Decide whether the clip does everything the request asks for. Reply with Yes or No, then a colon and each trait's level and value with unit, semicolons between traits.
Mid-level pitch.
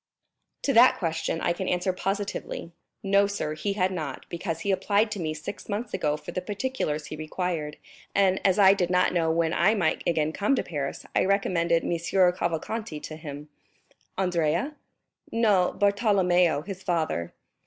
Yes: medium, 180 Hz